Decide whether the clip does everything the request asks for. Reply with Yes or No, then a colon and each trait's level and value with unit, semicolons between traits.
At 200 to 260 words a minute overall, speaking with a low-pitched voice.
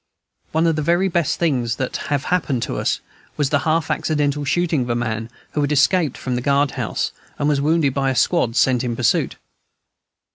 No: fast, 205 wpm; medium, 145 Hz